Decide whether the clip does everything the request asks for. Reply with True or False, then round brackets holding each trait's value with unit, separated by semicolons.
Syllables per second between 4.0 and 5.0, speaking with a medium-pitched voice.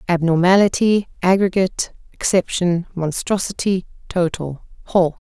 True (4.7 syllables/s; 180 Hz)